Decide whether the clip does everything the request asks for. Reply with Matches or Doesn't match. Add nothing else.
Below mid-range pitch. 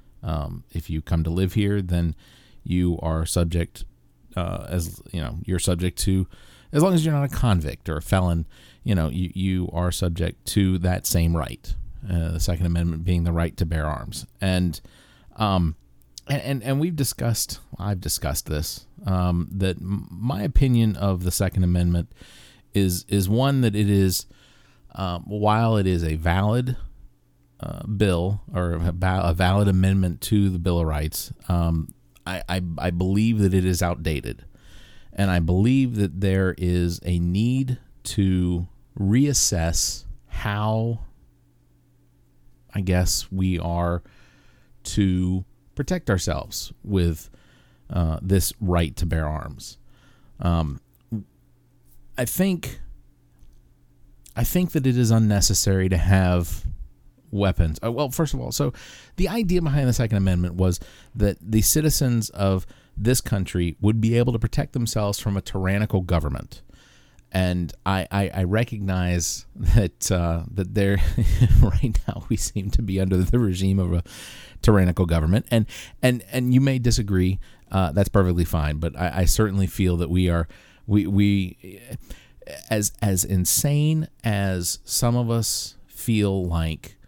Matches